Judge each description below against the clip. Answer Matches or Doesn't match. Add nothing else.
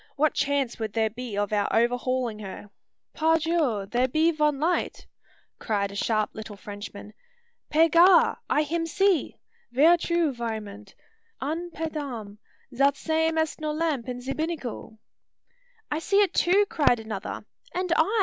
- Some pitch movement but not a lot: Doesn't match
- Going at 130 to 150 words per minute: Doesn't match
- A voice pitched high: Matches